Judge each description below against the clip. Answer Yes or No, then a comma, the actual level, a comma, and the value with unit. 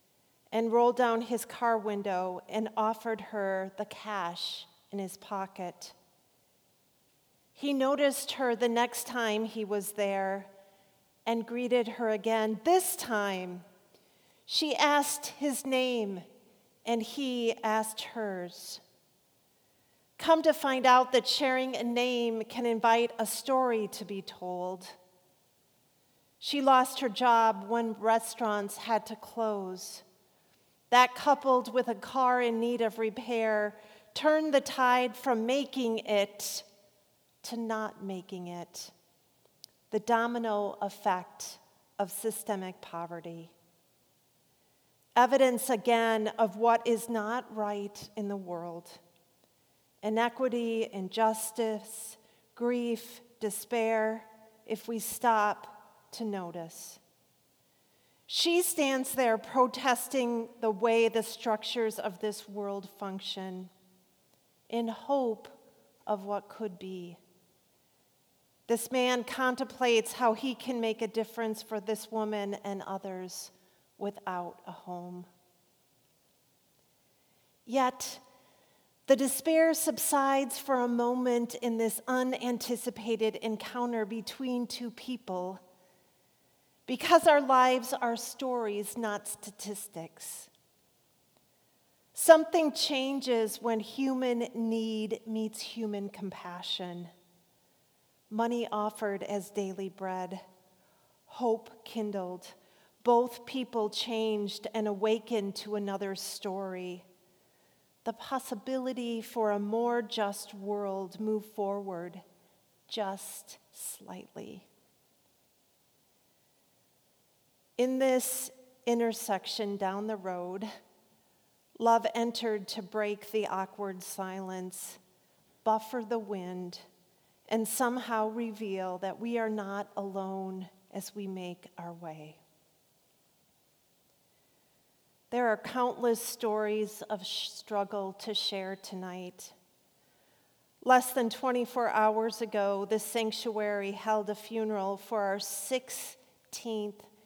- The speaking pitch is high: Yes, high, 220 Hz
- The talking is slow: Yes, slow, 100 wpm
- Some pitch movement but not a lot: Yes, average, 3.2 semitones